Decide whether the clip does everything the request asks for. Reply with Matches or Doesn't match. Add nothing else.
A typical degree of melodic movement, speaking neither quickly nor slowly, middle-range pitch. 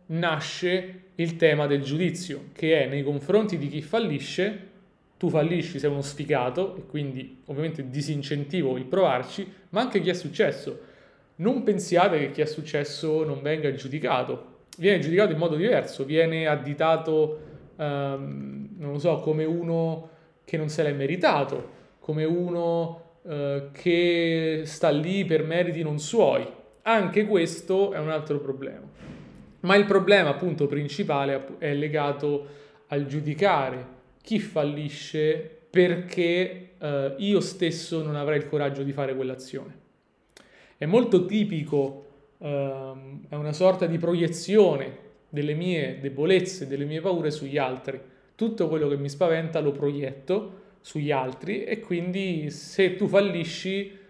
Matches